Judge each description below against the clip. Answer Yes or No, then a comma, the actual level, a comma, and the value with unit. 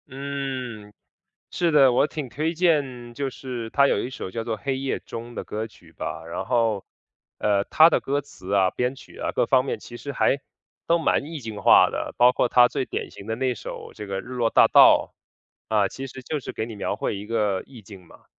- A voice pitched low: Yes, low, 125 Hz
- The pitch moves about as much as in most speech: Yes, average, 4.0 semitones